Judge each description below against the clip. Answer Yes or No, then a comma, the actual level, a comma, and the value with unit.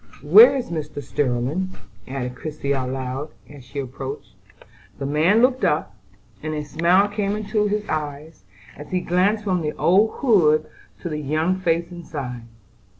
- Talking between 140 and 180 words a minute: Yes, average, 150 wpm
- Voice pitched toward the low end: No, medium, 155 Hz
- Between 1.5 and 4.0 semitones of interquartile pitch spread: No, average, 5.1 semitones